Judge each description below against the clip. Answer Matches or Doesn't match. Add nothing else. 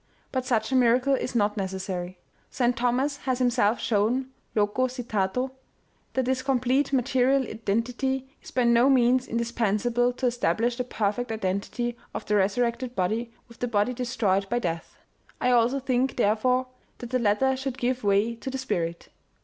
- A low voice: Doesn't match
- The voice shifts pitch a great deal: Doesn't match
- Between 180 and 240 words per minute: Doesn't match